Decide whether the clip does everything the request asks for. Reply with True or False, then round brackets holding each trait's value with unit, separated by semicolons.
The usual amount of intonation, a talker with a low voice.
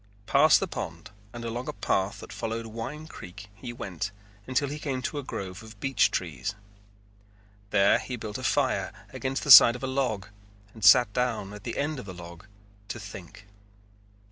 True (4.6 semitones; 110 Hz)